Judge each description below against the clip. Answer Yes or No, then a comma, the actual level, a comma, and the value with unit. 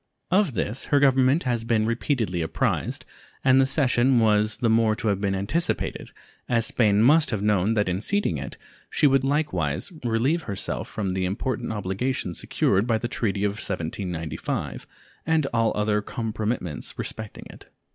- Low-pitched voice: Yes, low, 110 Hz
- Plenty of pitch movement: No, average, 4.5 semitones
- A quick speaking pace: No, average, 160 wpm